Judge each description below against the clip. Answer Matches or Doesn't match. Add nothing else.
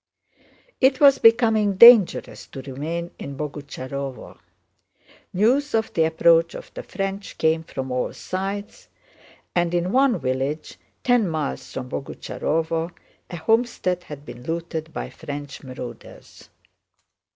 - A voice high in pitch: Doesn't match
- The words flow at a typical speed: Doesn't match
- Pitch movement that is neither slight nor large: Doesn't match